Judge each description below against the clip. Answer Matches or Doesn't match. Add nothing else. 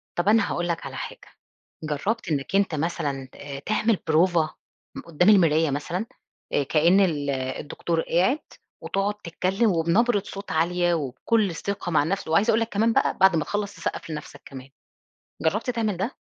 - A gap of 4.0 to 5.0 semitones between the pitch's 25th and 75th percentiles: Matches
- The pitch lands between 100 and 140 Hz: Doesn't match